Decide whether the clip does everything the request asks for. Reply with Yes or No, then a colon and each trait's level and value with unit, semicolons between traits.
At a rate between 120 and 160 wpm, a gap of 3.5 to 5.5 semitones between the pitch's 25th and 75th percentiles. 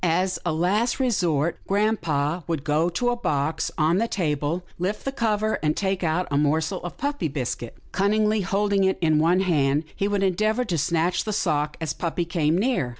No: average, 190 wpm; average, 4.7 semitones